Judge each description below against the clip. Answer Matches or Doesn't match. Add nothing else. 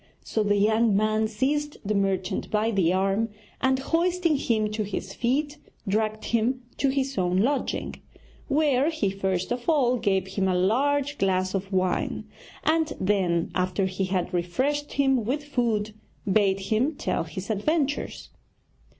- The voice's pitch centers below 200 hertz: Doesn't match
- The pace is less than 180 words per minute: Matches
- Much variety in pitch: Matches